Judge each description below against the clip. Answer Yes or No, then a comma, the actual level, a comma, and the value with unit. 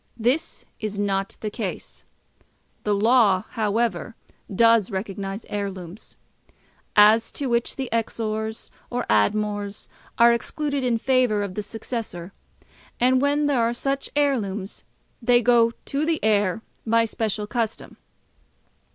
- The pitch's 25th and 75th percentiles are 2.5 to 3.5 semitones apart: Yes, average, 3.0 semitones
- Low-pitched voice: No, high, 225 Hz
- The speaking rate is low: Yes, slow, 125 wpm